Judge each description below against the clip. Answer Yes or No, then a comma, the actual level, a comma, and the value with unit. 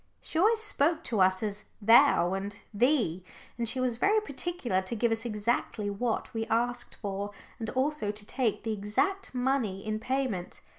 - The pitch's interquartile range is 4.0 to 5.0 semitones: Yes, average, 4.4 semitones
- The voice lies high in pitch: Yes, high, 230 Hz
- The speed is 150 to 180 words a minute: Yes, average, 170 wpm